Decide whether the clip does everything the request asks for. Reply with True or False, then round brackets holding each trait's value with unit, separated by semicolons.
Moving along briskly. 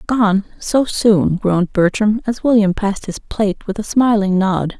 False (175 wpm)